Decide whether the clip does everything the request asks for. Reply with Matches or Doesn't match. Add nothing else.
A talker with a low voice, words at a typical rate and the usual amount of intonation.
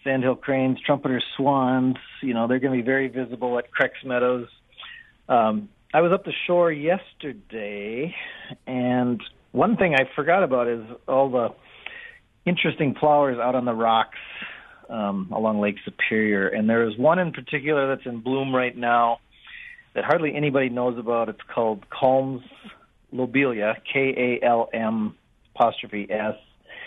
Matches